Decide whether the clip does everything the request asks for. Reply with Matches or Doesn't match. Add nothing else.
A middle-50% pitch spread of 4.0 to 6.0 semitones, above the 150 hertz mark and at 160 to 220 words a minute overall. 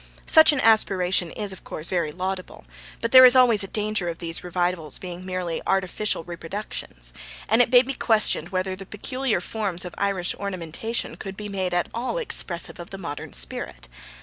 Doesn't match